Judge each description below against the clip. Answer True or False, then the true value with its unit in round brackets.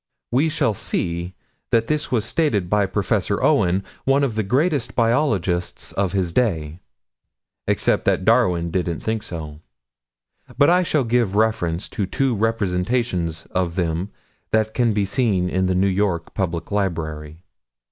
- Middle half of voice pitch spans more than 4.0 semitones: True (4.8 semitones)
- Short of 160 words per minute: True (145 wpm)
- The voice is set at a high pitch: False (100 Hz)